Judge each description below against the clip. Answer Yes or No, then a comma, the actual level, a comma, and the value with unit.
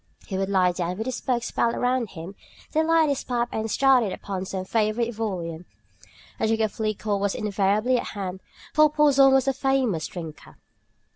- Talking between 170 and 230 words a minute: Yes, average, 190 wpm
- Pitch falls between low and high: No, high, 220 Hz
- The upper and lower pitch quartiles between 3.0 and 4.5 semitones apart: No, average, 5.1 semitones